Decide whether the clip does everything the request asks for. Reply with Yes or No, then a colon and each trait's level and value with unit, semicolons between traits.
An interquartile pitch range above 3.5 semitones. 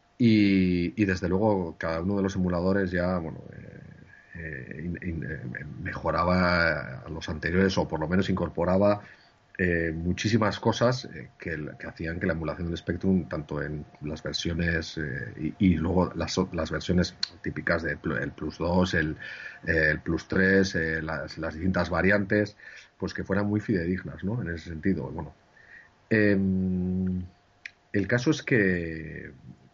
No: average, 3.0 semitones